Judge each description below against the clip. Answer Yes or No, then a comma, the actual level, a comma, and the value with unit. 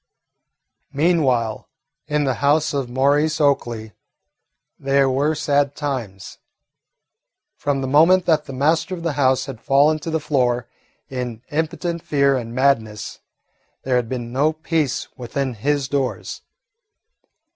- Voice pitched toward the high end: No, medium, 140 Hz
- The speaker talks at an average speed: No, slow, 130 wpm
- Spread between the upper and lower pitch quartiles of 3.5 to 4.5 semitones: No, average, 3.1 semitones